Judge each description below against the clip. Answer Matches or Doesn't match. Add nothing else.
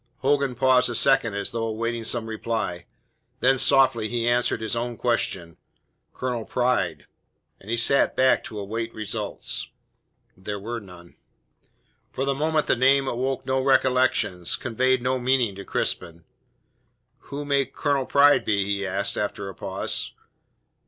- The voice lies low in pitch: Matches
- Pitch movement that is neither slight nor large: Matches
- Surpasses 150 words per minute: Doesn't match